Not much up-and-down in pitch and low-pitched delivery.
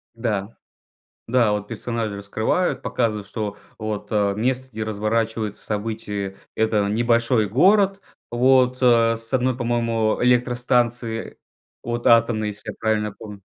Yes: narrow, 2.3 semitones; low, 115 Hz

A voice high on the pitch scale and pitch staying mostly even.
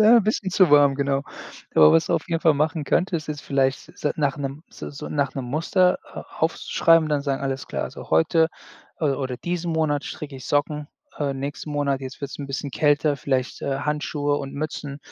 No: medium, 145 Hz; narrow, 2.3 semitones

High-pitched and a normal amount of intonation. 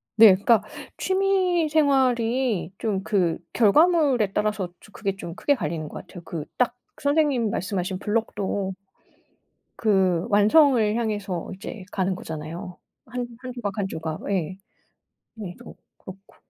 Yes: high, 210 Hz; average, 4.8 semitones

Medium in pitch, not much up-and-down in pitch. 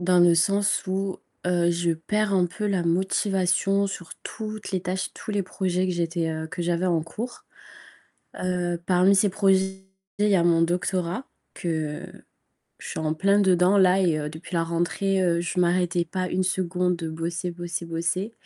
Yes: medium, 180 Hz; narrow, 2.1 semitones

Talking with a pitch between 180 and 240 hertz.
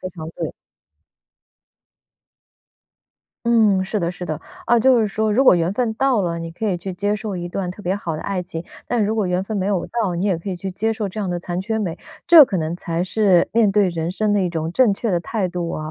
Yes: high, 190 Hz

